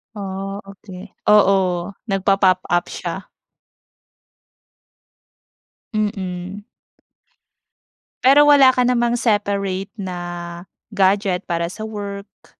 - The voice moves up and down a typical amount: No, narrow, 2.2 semitones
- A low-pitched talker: No, high, 200 Hz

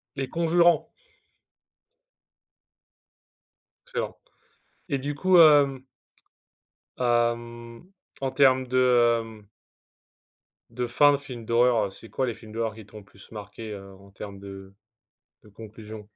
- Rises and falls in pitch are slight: No, average, 4.2 semitones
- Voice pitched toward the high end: No, low, 120 Hz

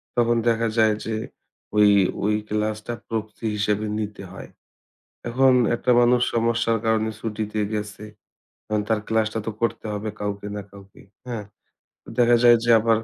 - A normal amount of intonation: No, narrow, 1.7 semitones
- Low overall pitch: Yes, low, 110 Hz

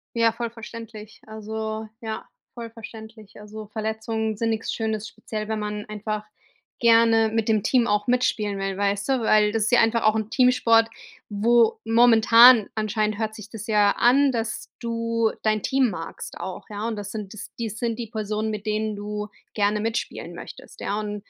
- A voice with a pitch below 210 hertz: No, high, 220 Hz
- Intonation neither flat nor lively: No, narrow, 1.5 semitones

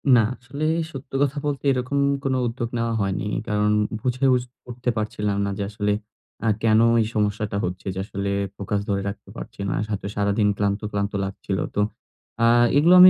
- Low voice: Yes, low, 105 Hz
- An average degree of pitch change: Yes, average, 3.5 semitones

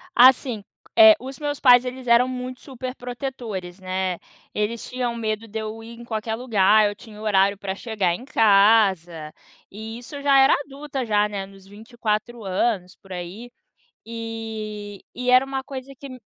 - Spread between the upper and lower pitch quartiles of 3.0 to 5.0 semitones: Yes, average, 3.7 semitones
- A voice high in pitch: Yes, high, 225 Hz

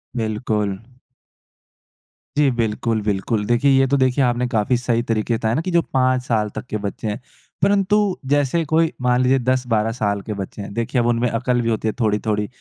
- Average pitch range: Yes, average, 3.1 semitones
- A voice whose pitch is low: Yes, low, 120 Hz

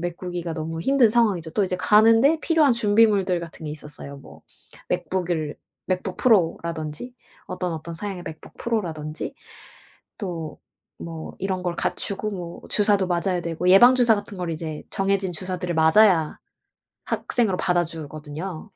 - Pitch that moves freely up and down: No, average, 4.0 semitones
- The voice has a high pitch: No, medium, 180 Hz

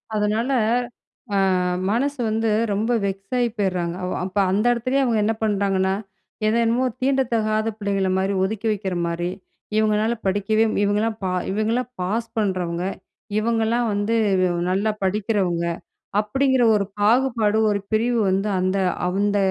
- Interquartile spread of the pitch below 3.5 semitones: Yes, average, 2.8 semitones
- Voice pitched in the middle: No, high, 215 Hz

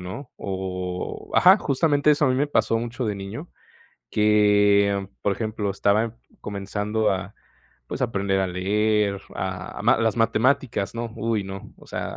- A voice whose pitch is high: No, low, 105 Hz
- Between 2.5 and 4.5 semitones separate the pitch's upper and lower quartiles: Yes, average, 2.9 semitones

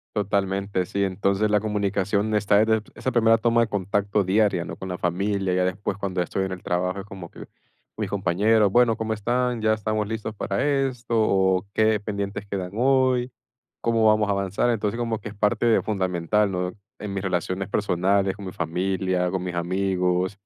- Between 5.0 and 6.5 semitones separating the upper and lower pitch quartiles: No, narrow, 2.6 semitones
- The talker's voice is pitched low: Yes, low, 100 Hz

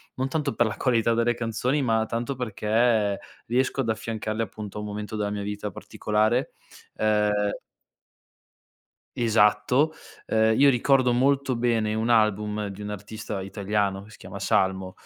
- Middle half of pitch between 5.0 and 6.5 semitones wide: No, narrow, 2.5 semitones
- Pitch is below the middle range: Yes, low, 110 Hz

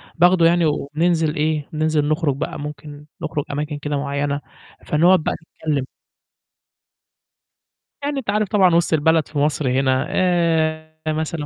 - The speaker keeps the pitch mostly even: Yes, narrow, 2.3 semitones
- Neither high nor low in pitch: Yes, medium, 155 Hz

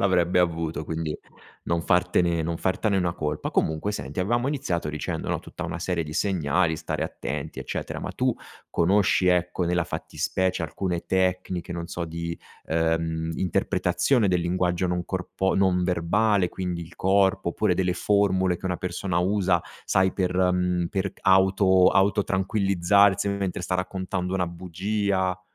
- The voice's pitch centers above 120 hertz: No, very low, 90 Hz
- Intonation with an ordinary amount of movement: No, narrow, 1.8 semitones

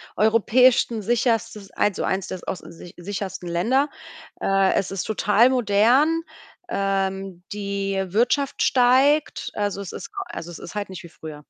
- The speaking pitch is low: No, high, 200 Hz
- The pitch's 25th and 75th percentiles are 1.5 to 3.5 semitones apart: No, average, 4.0 semitones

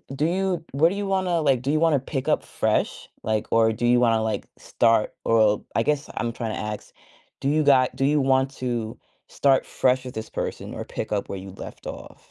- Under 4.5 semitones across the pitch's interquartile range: No, average, 4.8 semitones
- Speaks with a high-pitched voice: No, low, 130 Hz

